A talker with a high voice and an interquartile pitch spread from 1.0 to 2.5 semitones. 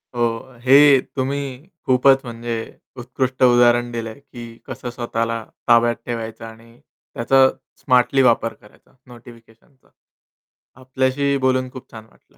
No: low, 120 Hz; narrow, 2.1 semitones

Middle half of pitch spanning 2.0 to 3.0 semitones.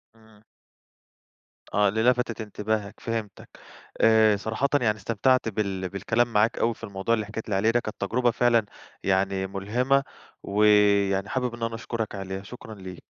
Yes: narrow, 2.6 semitones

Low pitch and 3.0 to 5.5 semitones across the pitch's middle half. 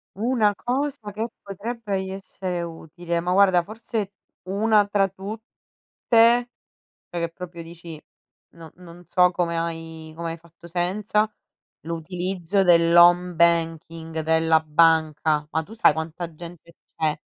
No: medium, 175 Hz; average, 3.3 semitones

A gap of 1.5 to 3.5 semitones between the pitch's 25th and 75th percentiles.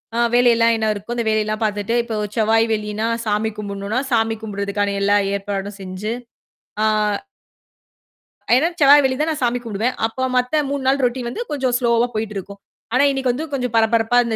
Yes: average, 3.0 semitones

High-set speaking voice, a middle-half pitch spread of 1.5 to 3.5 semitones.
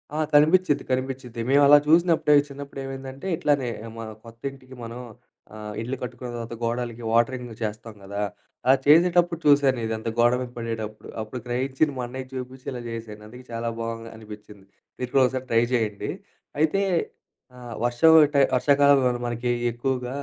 No: low, 125 Hz; average, 3.0 semitones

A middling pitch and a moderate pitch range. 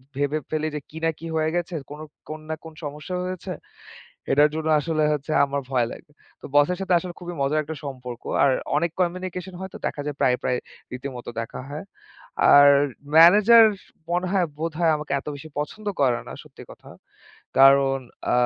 Yes: medium, 155 Hz; average, 3.7 semitones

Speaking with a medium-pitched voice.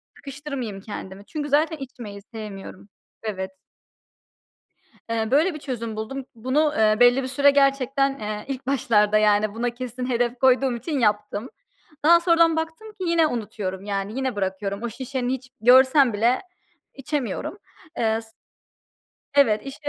No: high, 245 Hz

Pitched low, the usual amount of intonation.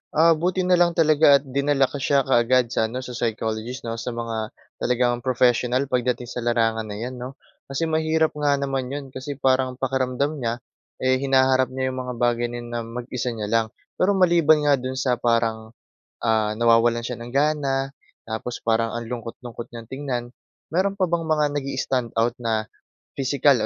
Yes: low, 125 Hz; average, 3.0 semitones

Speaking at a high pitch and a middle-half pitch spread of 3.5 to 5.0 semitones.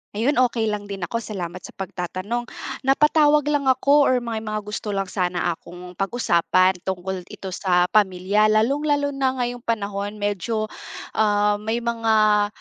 Yes: high, 210 Hz; average, 4.0 semitones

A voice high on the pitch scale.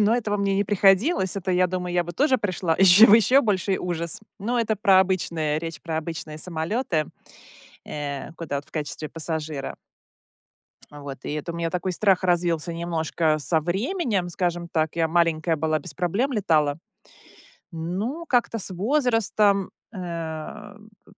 No: medium, 175 Hz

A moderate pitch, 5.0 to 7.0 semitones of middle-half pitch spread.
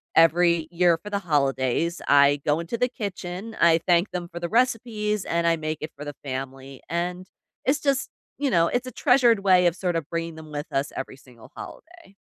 Yes: medium, 170 Hz; average, 5.3 semitones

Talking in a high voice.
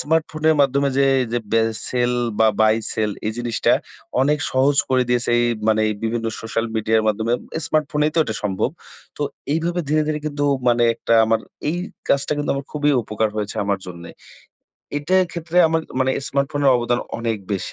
No: low, 130 Hz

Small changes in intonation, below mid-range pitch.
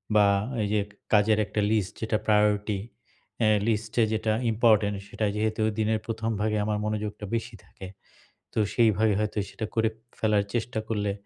Yes: narrow, 1.1 semitones; low, 110 Hz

